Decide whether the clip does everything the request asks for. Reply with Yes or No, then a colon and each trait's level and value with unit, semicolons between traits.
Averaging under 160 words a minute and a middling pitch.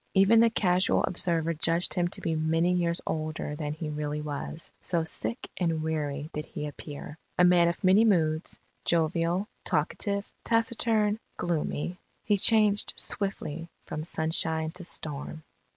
Yes: average, 145 wpm; medium, 165 Hz